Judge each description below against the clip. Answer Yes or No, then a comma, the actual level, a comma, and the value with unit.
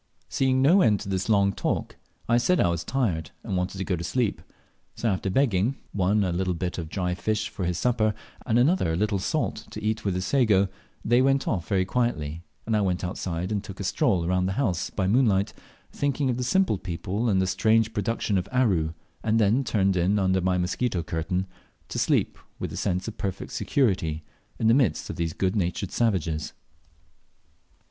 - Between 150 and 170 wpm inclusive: No, average, 200 wpm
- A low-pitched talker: Yes, low, 100 Hz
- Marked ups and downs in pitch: No, average, 4.0 semitones